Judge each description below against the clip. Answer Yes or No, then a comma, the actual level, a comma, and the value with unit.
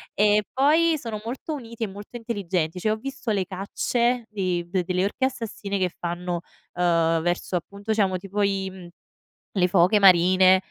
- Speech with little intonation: No, average, 3.8 semitones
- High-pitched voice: Yes, high, 195 Hz